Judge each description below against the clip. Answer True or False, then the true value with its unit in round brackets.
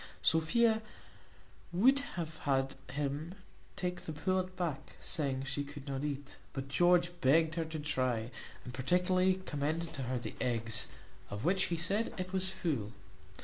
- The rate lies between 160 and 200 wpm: False (150 wpm)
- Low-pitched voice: False (160 Hz)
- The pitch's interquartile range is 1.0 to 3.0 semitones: False (4.9 semitones)